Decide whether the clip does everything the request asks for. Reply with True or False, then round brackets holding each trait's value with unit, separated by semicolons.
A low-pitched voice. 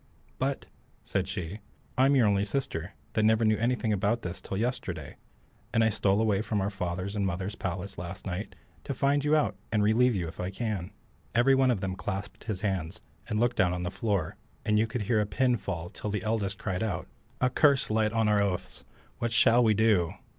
True (105 Hz)